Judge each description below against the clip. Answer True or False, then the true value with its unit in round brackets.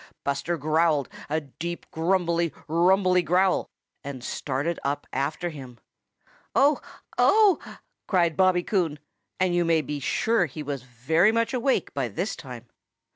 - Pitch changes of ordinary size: True (4.5 semitones)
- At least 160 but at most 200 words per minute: False (135 wpm)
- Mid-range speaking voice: True (165 Hz)